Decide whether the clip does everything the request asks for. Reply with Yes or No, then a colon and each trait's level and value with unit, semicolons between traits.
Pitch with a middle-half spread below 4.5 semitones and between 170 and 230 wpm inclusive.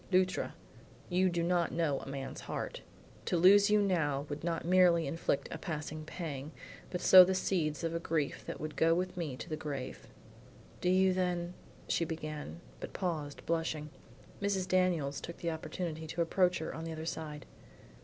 Yes: average, 2.9 semitones; average, 180 wpm